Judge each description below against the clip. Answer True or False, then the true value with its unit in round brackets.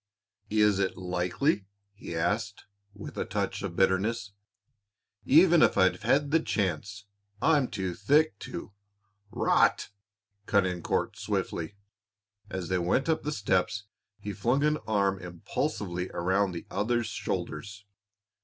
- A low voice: True (100 Hz)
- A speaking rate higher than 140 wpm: False (135 wpm)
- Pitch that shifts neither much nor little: True (4.0 semitones)